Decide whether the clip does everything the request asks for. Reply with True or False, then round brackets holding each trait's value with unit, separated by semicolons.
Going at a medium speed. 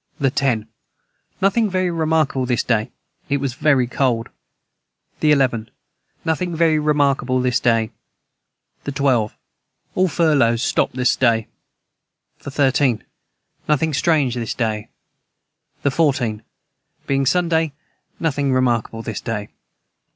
False (115 wpm)